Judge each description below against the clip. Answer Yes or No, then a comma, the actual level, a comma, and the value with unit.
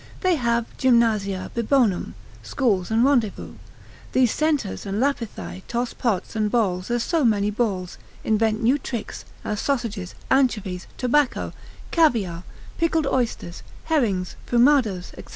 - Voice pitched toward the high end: Yes, high, 230 Hz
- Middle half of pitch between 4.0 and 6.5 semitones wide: Yes, average, 4.6 semitones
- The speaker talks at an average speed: No, slow, 125 wpm